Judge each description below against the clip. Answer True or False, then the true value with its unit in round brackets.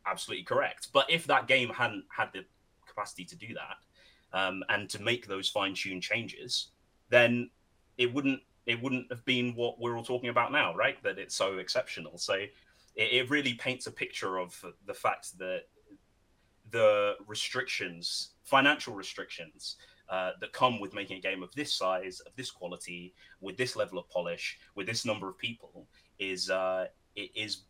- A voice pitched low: True (110 Hz)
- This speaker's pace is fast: False (175 wpm)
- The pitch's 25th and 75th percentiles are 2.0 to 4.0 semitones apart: False (5.0 semitones)